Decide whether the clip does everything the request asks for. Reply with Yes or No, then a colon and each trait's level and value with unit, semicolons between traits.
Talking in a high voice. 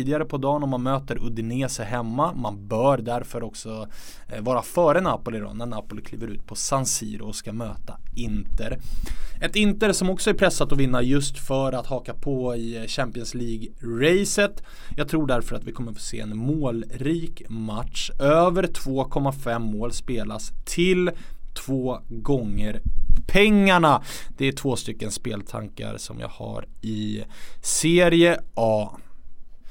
No: low, 120 Hz